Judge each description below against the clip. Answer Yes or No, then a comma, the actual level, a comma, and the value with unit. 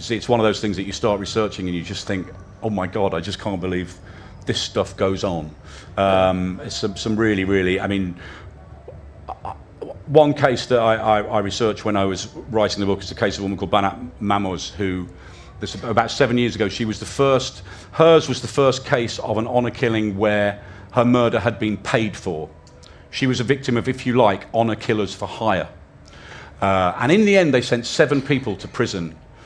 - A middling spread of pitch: Yes, average, 4.0 semitones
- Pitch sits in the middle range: No, low, 105 Hz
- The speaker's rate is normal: No, fast, 210 wpm